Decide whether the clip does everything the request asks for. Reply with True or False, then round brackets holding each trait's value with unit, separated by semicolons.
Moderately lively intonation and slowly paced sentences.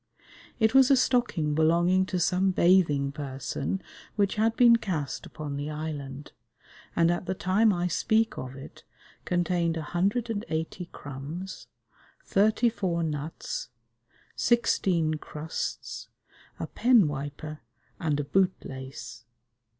True (4.9 semitones; 125 wpm)